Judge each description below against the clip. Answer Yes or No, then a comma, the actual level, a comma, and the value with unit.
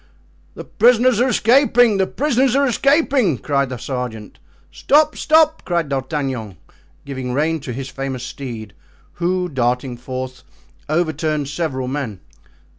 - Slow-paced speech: Yes, slow, 125 wpm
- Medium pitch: Yes, medium, 145 Hz